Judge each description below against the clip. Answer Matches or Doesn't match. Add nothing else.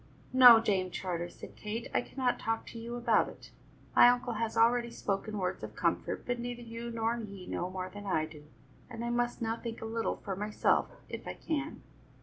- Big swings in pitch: Doesn't match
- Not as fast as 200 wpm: Doesn't match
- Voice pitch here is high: Matches